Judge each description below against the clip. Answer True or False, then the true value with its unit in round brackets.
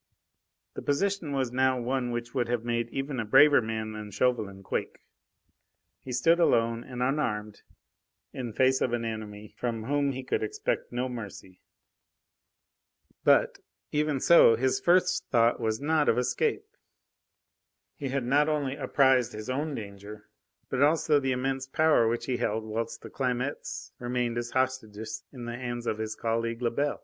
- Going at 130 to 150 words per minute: False (160 wpm)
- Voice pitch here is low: True (125 Hz)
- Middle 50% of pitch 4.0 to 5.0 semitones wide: False (3.1 semitones)